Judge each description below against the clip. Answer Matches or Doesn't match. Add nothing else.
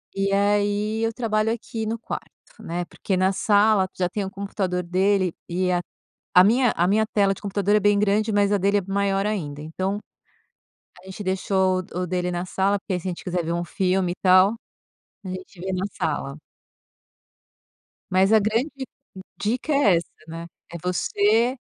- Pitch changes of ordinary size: Doesn't match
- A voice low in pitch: Doesn't match